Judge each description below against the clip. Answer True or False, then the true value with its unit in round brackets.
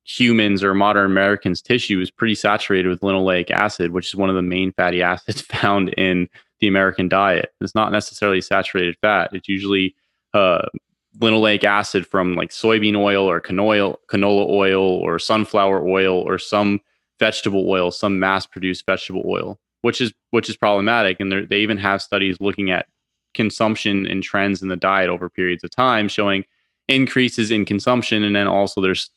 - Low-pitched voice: True (100 Hz)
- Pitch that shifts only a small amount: True (2.0 semitones)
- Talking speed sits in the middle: True (170 wpm)